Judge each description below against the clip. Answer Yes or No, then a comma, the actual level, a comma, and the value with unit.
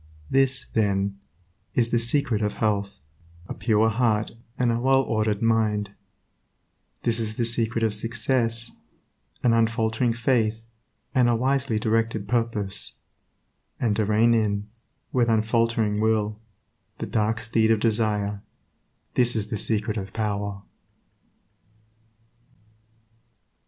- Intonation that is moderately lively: No, narrow, 1.7 semitones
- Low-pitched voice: Yes, low, 110 Hz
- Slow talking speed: Yes, slow, 120 wpm